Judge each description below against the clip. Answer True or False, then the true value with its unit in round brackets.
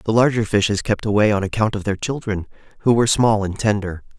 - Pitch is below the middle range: True (105 Hz)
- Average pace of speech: False (215 wpm)